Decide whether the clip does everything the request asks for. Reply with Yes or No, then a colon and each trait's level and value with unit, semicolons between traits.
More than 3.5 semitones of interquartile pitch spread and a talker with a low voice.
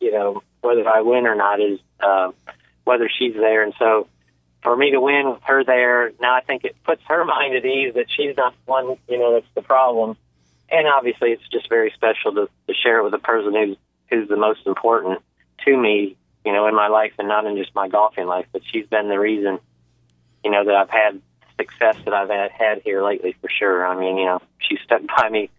Yes: average, 4.3 semitones; low, 110 Hz